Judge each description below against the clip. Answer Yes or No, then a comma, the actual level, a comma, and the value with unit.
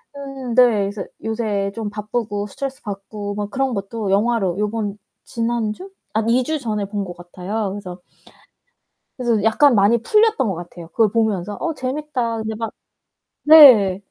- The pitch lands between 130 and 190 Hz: No, high, 220 Hz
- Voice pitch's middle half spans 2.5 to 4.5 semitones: Yes, average, 3.2 semitones